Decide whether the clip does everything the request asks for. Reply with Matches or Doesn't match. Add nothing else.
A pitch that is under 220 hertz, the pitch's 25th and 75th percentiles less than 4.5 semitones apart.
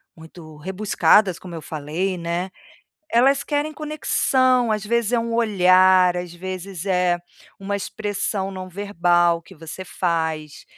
Matches